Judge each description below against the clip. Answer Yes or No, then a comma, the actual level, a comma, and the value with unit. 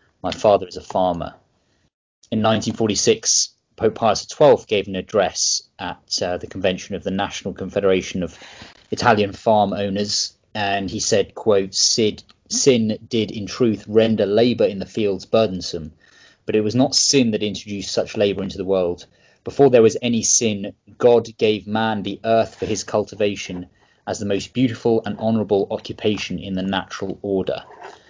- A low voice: Yes, low, 105 Hz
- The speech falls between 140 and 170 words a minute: Yes, average, 160 wpm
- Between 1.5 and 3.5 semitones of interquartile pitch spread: Yes, narrow, 2.4 semitones